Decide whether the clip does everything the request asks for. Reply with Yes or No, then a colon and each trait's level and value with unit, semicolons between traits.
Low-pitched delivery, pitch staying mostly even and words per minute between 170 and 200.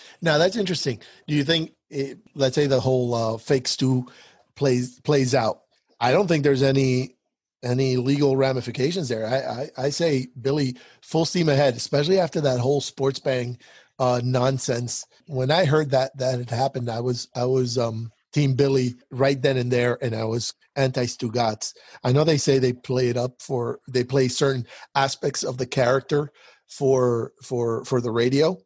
Yes: low, 130 Hz; narrow, 2.2 semitones; average, 180 wpm